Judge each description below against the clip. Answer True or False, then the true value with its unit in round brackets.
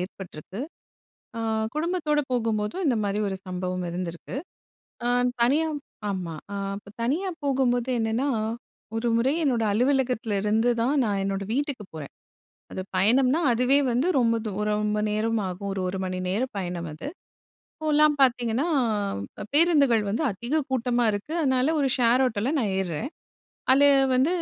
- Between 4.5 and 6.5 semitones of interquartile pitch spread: True (5.1 semitones)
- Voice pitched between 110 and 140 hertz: False (235 Hz)